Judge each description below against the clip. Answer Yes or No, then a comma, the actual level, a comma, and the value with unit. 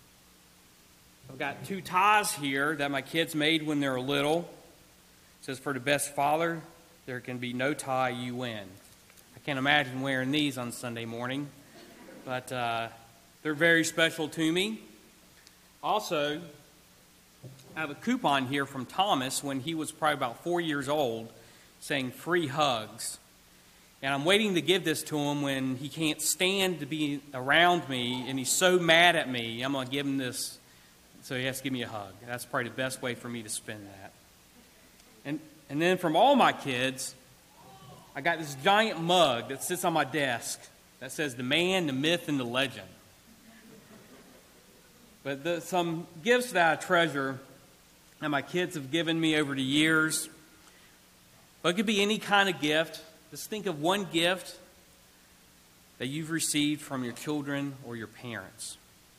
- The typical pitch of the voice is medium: Yes, medium, 145 Hz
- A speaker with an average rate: Yes, average, 170 wpm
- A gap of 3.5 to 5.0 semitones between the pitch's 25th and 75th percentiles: Yes, average, 4.4 semitones